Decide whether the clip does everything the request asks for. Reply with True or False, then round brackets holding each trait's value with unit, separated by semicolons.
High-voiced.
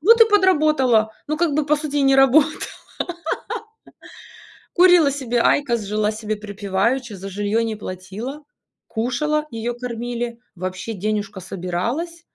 True (240 Hz)